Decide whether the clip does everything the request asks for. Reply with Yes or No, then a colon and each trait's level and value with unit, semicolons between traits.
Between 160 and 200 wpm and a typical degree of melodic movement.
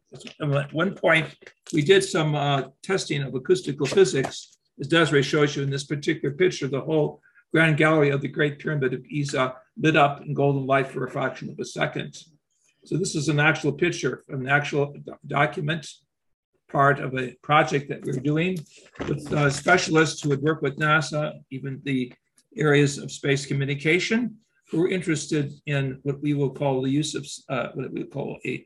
No: average, 180 wpm; narrow, 2.2 semitones